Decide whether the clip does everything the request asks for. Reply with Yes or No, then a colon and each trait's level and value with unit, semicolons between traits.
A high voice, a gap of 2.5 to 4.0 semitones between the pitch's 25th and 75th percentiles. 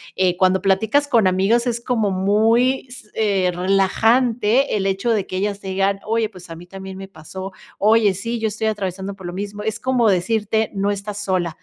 Yes: high, 200 Hz; average, 2.8 semitones